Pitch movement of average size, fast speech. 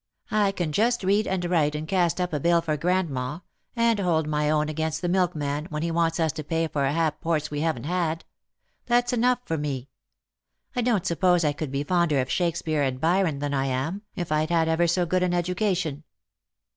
Yes: average, 3.1 semitones; fast, 210 wpm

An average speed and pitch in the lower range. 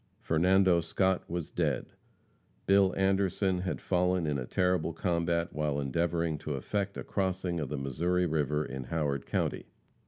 Yes: average, 150 wpm; very low, 85 Hz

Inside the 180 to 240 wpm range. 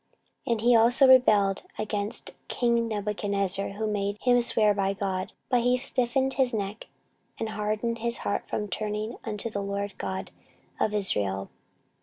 No: average, 160 wpm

